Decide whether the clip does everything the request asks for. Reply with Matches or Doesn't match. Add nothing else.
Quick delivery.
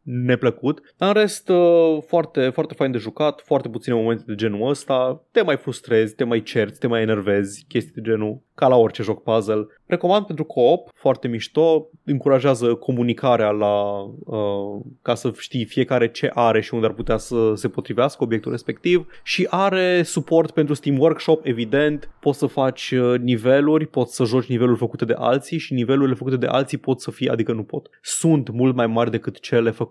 Matches